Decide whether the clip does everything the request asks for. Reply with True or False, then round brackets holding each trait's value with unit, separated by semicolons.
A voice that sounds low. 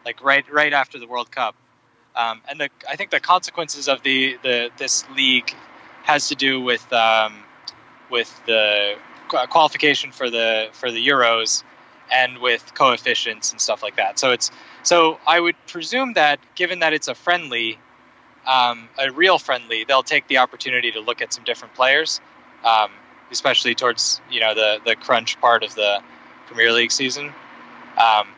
True (130 Hz)